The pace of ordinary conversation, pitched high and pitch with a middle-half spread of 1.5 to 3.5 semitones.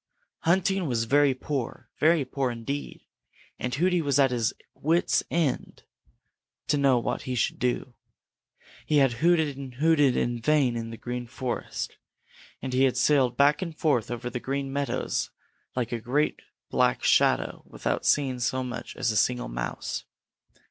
No: average, 160 wpm; low, 130 Hz; average, 3.2 semitones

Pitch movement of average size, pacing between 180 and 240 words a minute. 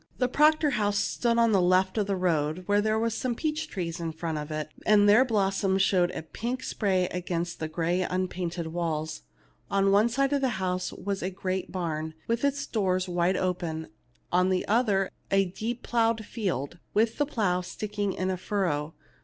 Yes: average, 3.9 semitones; average, 190 wpm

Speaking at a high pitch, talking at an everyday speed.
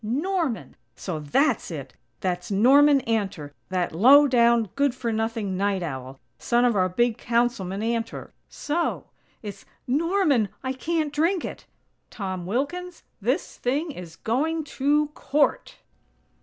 No: high, 235 Hz; slow, 130 wpm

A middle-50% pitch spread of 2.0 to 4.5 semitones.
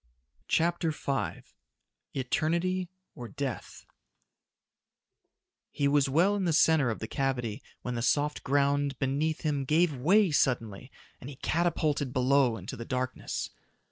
Yes: average, 3.8 semitones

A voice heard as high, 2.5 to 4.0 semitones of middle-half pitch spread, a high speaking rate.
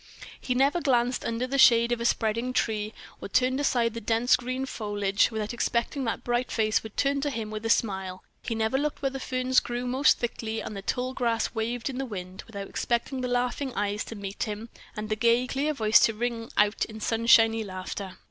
Yes: high, 230 Hz; average, 2.8 semitones; fast, 215 wpm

